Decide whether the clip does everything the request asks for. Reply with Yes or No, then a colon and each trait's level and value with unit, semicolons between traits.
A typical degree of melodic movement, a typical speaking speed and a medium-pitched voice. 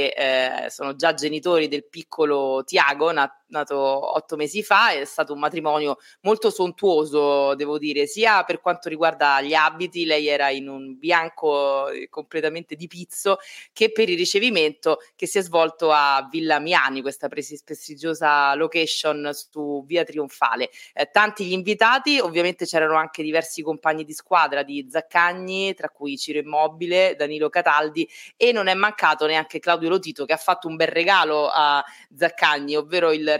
Yes: average, 3.1 semitones; average, 155 wpm; medium, 155 Hz